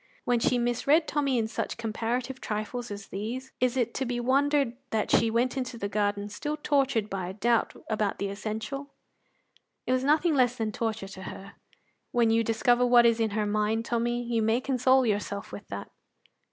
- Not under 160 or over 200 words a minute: Yes, average, 190 wpm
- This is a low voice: No, high, 235 Hz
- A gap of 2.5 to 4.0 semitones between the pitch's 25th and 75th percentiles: Yes, average, 3.1 semitones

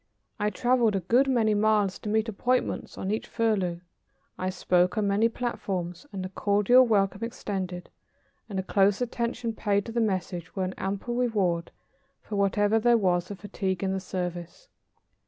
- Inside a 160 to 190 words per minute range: Yes, average, 170 wpm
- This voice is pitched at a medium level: No, high, 205 Hz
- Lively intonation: No, average, 3.3 semitones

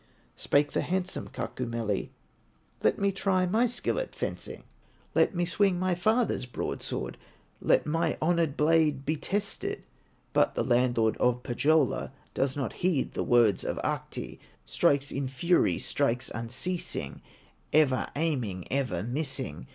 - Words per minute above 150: No, slow, 135 wpm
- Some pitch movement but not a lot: No, wide, 6.1 semitones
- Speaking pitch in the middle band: Yes, medium, 145 Hz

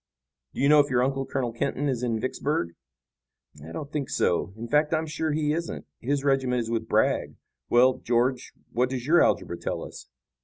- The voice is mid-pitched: No, low, 130 Hz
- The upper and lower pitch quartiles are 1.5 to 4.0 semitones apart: Yes, average, 3.4 semitones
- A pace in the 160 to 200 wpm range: Yes, average, 195 wpm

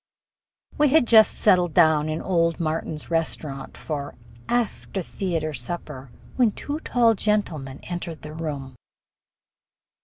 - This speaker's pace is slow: Yes, slow, 120 wpm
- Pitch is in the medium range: Yes, medium, 165 Hz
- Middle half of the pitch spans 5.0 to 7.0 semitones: Yes, wide, 5.5 semitones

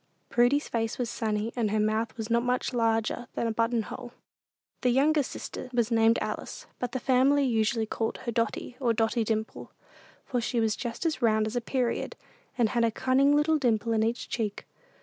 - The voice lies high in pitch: Yes, high, 235 Hz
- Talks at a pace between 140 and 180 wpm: No, average, 190 wpm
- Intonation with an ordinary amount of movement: No, narrow, 2.1 semitones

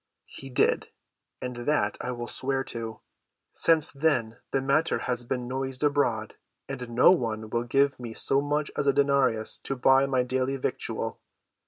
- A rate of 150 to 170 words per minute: Yes, average, 165 wpm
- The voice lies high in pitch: No, low, 130 Hz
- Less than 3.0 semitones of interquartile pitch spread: Yes, narrow, 2.6 semitones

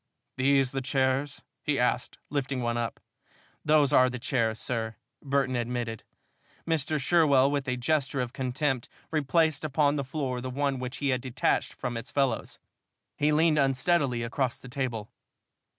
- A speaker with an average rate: Yes, average, 155 wpm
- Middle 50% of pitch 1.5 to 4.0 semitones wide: Yes, narrow, 2.4 semitones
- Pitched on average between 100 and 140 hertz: Yes, low, 135 Hz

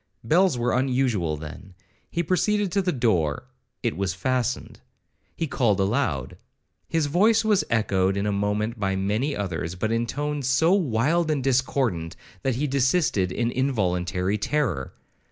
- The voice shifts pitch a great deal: Yes, wide, 6.9 semitones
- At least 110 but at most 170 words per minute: Yes, average, 140 wpm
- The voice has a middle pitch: No, low, 120 Hz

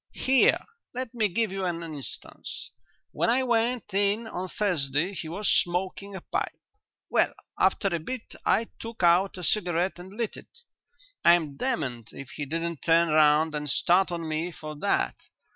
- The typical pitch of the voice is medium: Yes, medium, 180 Hz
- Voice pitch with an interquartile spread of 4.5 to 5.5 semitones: Yes, average, 4.8 semitones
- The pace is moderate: Yes, average, 165 wpm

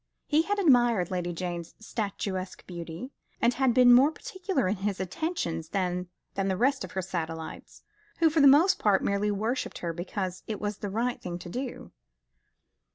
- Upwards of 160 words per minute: Yes, average, 170 wpm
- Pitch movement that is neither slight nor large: No, wide, 6.1 semitones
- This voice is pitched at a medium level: No, high, 205 Hz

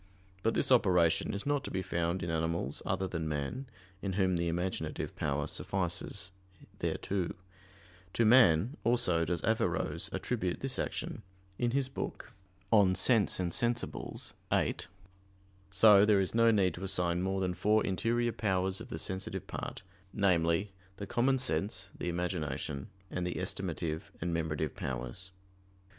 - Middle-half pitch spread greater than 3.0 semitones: Yes, average, 4.2 semitones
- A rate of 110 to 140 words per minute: No, average, 150 wpm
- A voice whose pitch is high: No, very low, 95 Hz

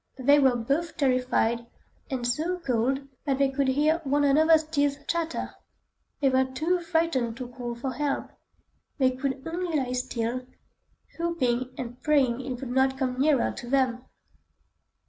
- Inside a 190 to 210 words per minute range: No, average, 150 wpm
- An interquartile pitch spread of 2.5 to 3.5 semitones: Yes, average, 2.8 semitones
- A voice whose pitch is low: No, very high, 265 Hz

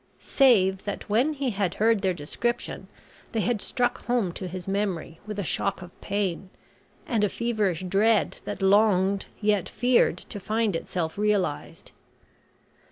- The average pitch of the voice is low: No, high, 205 Hz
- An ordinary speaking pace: Yes, average, 150 wpm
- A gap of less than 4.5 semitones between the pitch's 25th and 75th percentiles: Yes, average, 3.2 semitones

